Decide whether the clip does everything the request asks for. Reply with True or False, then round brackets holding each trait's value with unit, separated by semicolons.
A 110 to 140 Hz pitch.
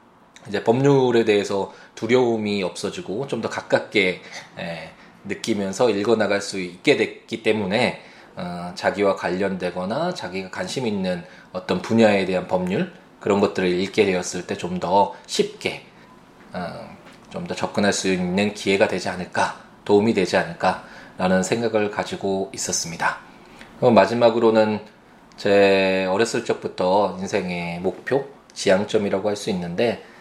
False (100 Hz)